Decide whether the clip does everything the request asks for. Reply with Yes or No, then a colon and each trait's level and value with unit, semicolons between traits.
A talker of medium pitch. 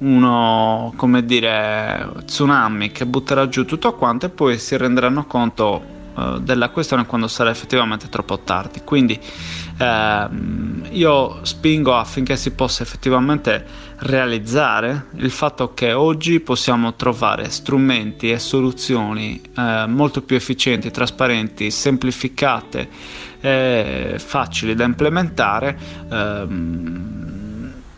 No: low, 125 Hz